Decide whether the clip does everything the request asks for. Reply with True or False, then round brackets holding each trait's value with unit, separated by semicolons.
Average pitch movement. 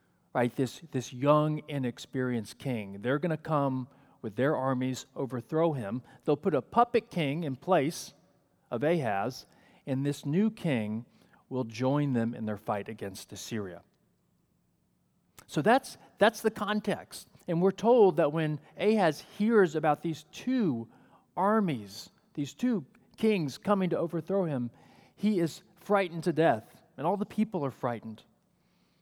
False (7.1 semitones)